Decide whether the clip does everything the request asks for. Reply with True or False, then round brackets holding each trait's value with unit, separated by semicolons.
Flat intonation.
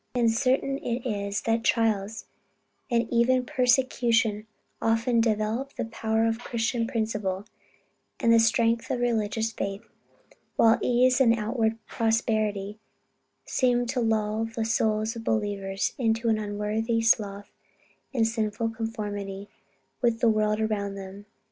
True (1.7 semitones)